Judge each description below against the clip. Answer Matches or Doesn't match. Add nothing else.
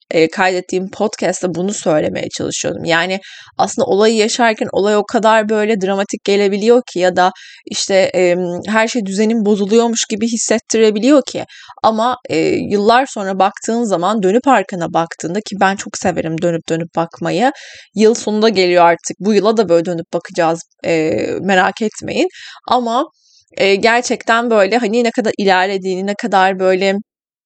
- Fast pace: Matches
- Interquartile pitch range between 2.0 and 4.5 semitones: Matches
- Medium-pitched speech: Doesn't match